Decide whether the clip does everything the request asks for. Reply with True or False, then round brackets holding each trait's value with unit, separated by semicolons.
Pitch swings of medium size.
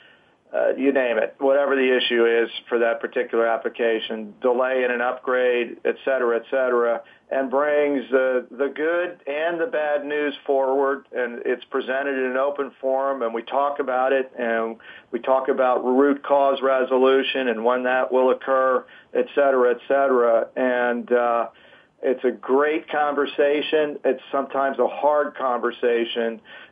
False (2.3 semitones)